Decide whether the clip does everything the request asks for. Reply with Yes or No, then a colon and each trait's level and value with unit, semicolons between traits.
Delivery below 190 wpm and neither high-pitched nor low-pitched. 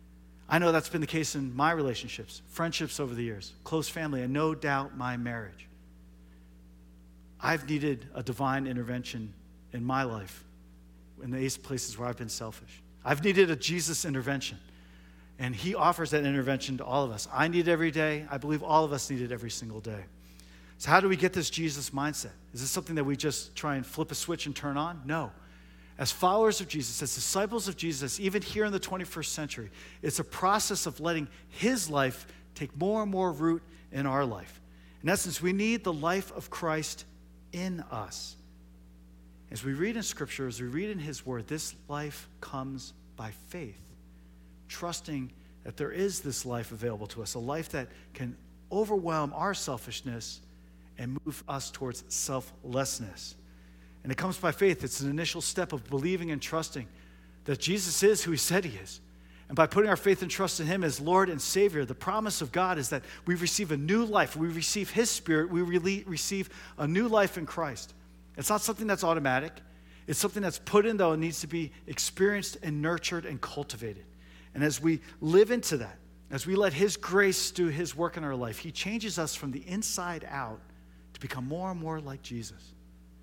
No: average, 195 wpm; medium, 145 Hz